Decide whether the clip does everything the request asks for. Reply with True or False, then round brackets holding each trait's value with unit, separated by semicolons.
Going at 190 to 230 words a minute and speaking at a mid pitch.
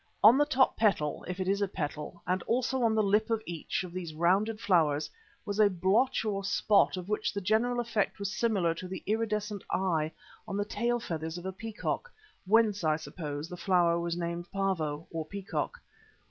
False (195 wpm; 195 Hz)